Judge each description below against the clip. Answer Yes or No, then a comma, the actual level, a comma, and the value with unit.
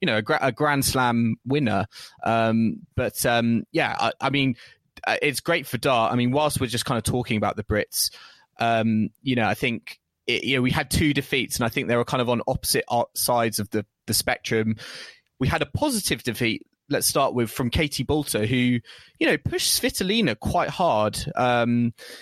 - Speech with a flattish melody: No, average, 3.6 semitones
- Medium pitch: No, low, 125 Hz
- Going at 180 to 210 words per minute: Yes, average, 195 wpm